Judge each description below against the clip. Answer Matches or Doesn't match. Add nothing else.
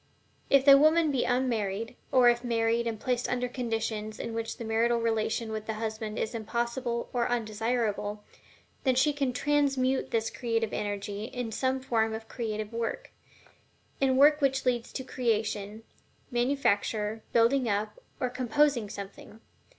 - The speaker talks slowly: Doesn't match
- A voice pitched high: Matches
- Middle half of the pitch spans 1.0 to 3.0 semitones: Matches